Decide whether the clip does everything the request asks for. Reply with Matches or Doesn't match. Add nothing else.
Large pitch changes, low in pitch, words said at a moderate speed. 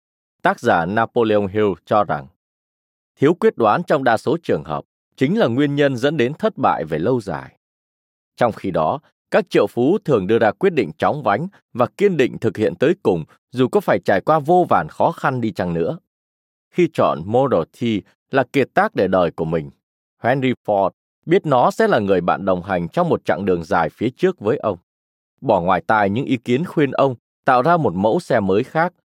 Matches